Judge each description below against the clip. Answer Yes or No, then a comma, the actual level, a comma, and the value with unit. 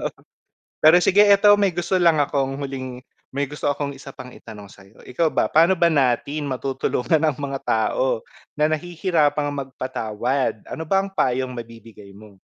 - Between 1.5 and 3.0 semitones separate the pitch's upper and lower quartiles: No, average, 4.2 semitones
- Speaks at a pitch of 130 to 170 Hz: Yes, medium, 140 Hz